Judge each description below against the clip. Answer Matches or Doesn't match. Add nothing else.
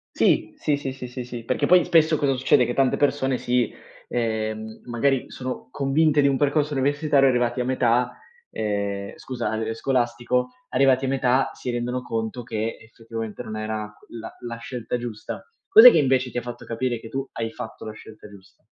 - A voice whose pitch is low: Matches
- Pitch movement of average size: Matches